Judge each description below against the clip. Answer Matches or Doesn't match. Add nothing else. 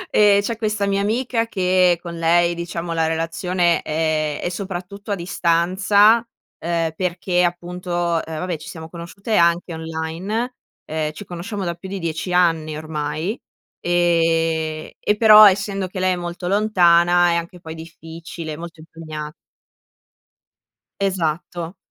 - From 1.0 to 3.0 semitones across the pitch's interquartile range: Matches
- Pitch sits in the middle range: Matches